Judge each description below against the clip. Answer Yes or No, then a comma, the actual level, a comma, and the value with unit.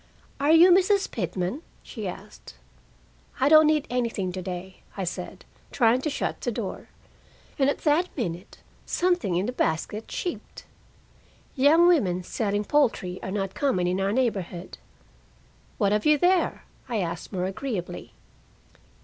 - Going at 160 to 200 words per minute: No, average, 145 wpm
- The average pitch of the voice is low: No, high, 220 Hz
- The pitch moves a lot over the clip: Yes, wide, 8.0 semitones